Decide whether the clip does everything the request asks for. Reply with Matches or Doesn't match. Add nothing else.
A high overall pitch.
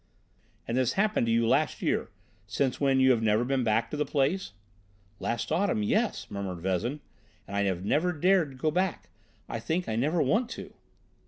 Doesn't match